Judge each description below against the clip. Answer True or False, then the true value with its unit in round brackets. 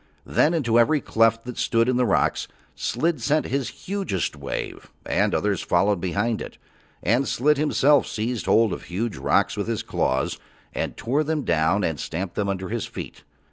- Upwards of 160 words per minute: True (180 wpm)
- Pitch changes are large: True (6.0 semitones)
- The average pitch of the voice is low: True (115 Hz)